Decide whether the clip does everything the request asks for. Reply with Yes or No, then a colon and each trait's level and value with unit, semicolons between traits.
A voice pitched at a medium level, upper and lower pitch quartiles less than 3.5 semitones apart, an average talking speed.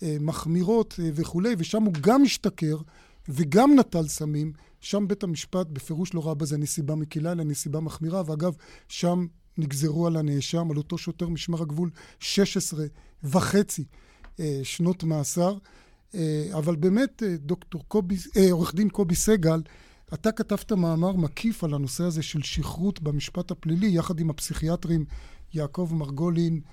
Yes: medium, 170 Hz; average, 3.0 semitones; average, 125 wpm